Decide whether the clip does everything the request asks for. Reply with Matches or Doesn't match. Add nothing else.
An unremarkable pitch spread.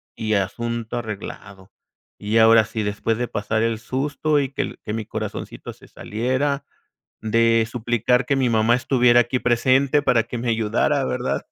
Doesn't match